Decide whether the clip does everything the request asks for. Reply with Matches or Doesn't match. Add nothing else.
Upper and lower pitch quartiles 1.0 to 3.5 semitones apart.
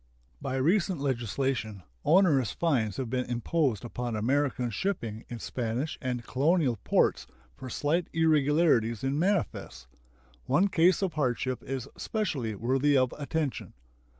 Doesn't match